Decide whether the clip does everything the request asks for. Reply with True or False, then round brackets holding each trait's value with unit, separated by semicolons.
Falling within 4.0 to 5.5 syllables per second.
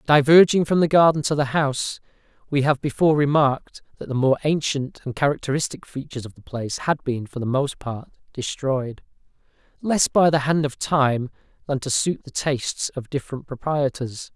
True (5.3 syllables/s)